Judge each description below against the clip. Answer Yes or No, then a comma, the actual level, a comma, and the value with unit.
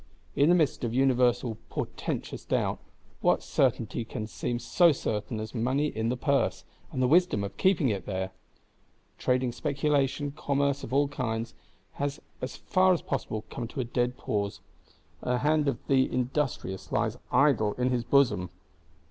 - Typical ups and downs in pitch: Yes, average, 3.9 semitones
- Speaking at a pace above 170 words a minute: No, average, 165 wpm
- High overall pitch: No, low, 125 Hz